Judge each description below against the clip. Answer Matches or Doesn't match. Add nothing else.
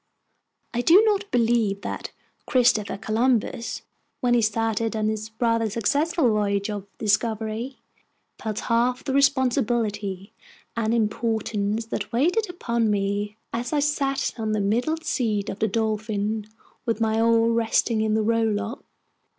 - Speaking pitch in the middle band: Doesn't match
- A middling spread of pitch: Doesn't match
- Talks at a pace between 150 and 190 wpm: Doesn't match